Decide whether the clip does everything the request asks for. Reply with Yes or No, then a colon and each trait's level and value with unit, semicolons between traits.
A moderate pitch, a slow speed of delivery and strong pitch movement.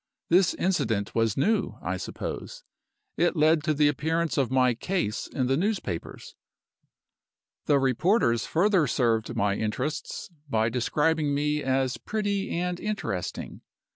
Yes: medium, 145 Hz; slow, 130 wpm; wide, 6.5 semitones